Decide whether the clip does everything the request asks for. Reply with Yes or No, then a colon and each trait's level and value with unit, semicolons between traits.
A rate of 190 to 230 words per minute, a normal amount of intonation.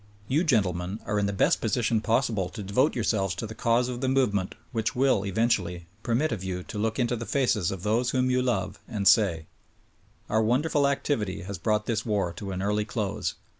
Yes: fast, 205 wpm; average, 4.0 semitones